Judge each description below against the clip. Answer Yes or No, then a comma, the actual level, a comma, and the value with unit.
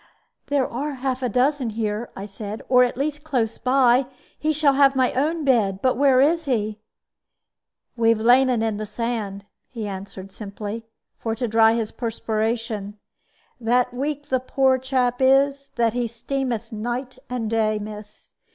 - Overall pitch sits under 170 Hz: No, high, 240 Hz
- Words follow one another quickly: No, average, 165 wpm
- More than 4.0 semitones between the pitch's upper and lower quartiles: No, average, 3.4 semitones